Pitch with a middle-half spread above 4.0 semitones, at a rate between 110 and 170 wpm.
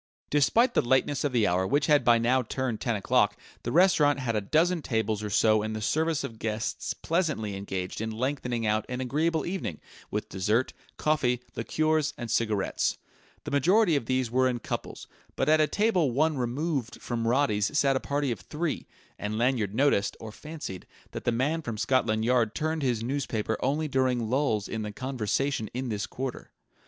No: average, 4.9 semitones; average, 185 wpm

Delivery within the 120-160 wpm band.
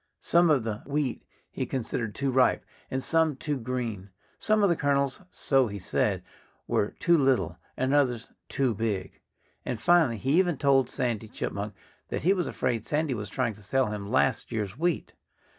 No: average, 175 wpm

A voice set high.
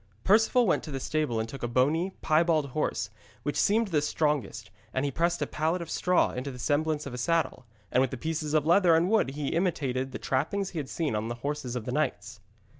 No: medium, 150 Hz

